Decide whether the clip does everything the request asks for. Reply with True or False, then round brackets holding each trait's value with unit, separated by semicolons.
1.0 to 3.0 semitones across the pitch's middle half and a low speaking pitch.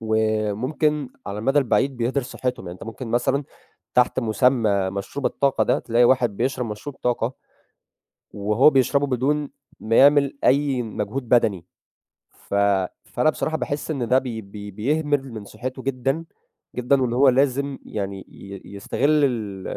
False (4.1 semitones; 125 Hz)